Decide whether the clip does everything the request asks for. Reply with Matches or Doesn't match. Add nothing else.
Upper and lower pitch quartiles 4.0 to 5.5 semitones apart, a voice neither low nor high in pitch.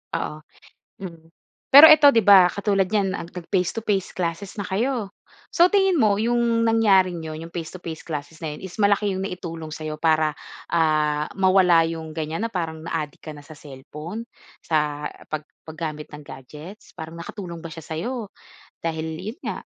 Matches